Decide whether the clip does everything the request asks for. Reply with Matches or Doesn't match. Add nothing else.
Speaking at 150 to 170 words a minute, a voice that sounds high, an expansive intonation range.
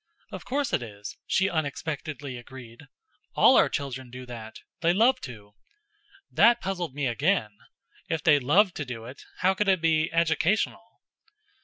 Doesn't match